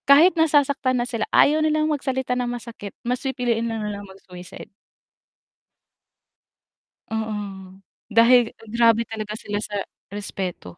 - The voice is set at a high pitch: Yes, high, 235 Hz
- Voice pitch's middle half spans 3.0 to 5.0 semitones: Yes, average, 3.9 semitones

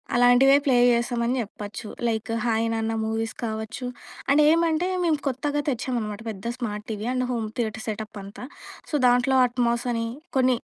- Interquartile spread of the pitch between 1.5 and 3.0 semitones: Yes, narrow, 2.6 semitones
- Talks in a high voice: Yes, high, 235 Hz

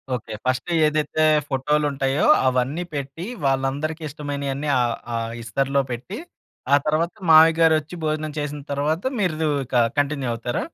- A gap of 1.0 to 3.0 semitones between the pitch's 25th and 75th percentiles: Yes, narrow, 2.6 semitones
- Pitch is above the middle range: No, medium, 145 Hz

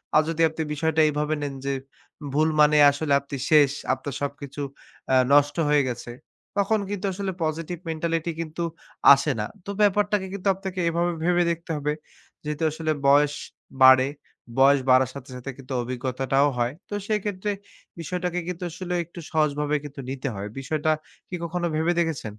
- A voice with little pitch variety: No, average, 3.7 semitones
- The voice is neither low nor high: Yes, medium, 150 Hz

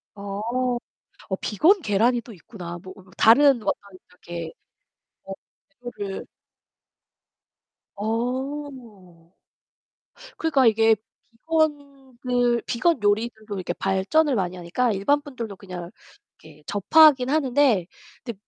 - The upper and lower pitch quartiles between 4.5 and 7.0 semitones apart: Yes, wide, 5.5 semitones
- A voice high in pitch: Yes, high, 225 Hz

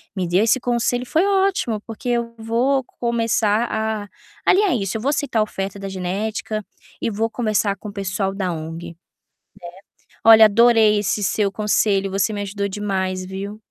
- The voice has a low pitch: No, high, 215 Hz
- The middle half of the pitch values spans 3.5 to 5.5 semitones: No, average, 2.9 semitones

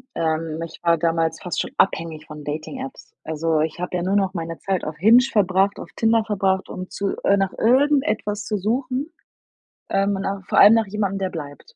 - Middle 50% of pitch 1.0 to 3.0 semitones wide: No, average, 4.3 semitones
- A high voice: Yes, high, 195 Hz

